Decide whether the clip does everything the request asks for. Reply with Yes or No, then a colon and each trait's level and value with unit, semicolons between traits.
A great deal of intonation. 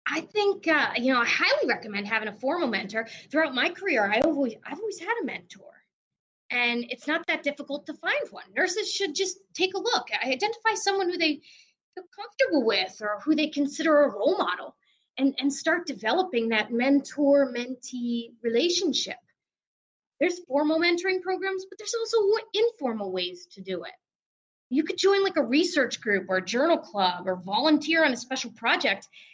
Yes: wide, 7.5 semitones